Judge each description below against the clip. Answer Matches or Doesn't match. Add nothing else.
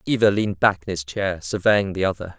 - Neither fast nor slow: Doesn't match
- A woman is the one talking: Doesn't match